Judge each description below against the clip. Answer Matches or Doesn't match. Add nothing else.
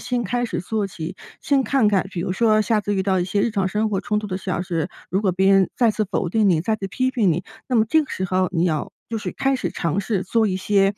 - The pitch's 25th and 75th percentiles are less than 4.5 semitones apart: Matches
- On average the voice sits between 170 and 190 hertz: Doesn't match